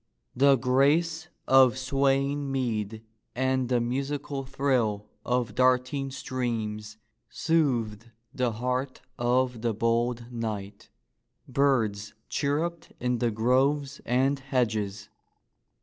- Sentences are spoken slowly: Yes, slow, 100 wpm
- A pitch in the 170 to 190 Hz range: No, low, 125 Hz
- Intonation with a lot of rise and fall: No, average, 2.9 semitones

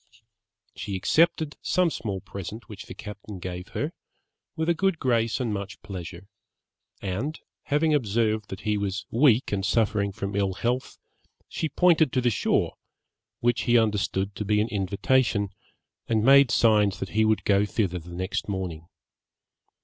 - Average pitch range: Yes, average, 4.1 semitones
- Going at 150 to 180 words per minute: Yes, average, 155 wpm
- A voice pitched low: Yes, low, 105 Hz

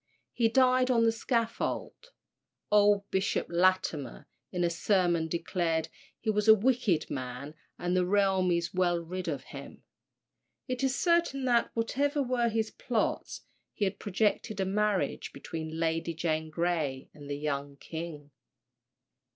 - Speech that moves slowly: No, average, 145 wpm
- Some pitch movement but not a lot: No, wide, 5.7 semitones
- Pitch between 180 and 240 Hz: Yes, medium, 185 Hz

